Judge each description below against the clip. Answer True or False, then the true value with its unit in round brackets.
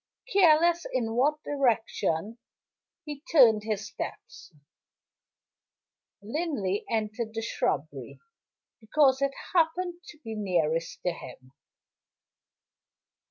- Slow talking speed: True (90 wpm)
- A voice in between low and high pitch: False (230 Hz)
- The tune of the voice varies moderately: False (6.4 semitones)